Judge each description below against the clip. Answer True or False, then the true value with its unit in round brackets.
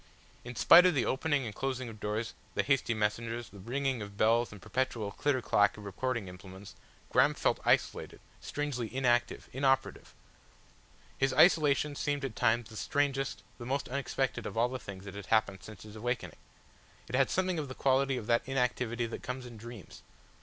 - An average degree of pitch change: True (3.7 semitones)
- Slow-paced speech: False (185 wpm)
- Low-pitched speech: True (120 Hz)